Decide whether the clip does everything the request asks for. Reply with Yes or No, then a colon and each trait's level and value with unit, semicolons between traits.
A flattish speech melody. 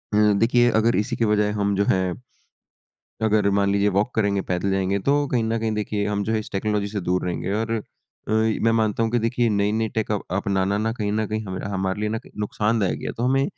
Yes: narrow, 2.0 semitones